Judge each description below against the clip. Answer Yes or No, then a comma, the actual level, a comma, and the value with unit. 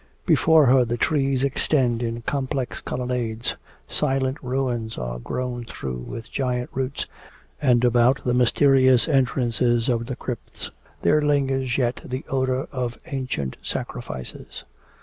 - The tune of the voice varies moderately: No, narrow, 2.0 semitones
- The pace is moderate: No, slow, 130 wpm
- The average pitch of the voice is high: No, low, 125 Hz